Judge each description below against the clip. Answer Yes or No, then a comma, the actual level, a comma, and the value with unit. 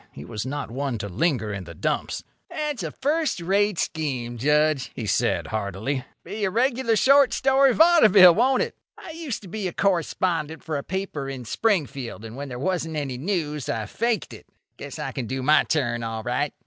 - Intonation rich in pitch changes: Yes, wide, 8.8 semitones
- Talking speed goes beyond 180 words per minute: Yes, average, 190 wpm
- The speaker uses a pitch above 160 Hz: No, medium, 155 Hz